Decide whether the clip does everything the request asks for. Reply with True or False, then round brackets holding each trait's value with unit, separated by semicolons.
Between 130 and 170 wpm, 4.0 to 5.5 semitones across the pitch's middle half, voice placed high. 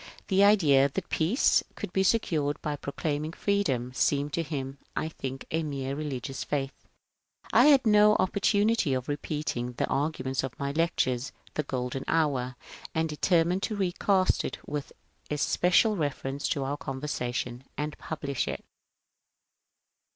False (150 wpm; 4.6 semitones; 150 Hz)